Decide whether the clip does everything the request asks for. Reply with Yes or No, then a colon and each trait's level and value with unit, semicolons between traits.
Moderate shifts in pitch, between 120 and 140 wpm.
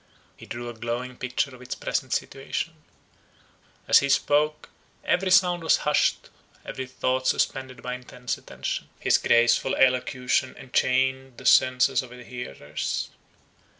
No: narrow, 1.2 semitones; slow, 135 wpm